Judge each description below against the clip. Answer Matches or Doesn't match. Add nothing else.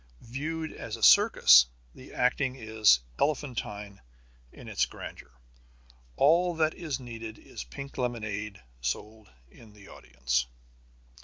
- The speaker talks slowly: Matches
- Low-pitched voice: Matches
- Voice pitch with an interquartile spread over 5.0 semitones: Matches